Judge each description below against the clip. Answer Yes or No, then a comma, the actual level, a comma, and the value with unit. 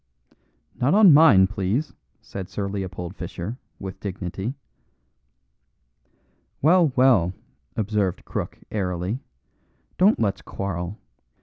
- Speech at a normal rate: No, slow, 95 wpm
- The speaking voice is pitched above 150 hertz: No, low, 100 Hz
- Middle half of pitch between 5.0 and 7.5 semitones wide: Yes, wide, 5.4 semitones